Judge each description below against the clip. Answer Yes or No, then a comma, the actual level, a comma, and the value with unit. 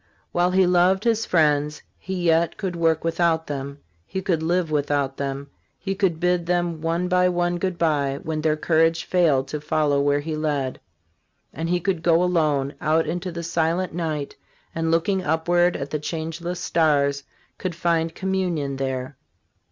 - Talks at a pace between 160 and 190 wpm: Yes, average, 165 wpm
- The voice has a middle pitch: Yes, medium, 165 Hz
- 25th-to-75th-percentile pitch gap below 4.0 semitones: Yes, average, 2.8 semitones